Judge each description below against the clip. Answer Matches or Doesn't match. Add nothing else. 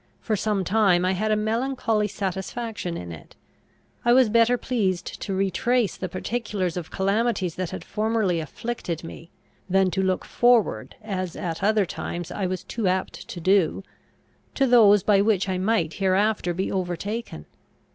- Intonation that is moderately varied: Matches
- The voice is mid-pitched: Doesn't match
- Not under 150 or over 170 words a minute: Matches